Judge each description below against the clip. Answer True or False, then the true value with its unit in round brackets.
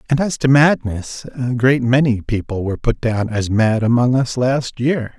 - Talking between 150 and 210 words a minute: True (195 wpm)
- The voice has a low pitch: True (125 Hz)